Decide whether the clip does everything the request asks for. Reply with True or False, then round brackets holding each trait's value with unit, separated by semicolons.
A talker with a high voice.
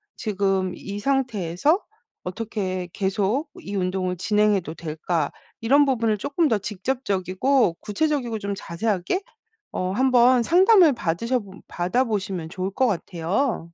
True (205 Hz)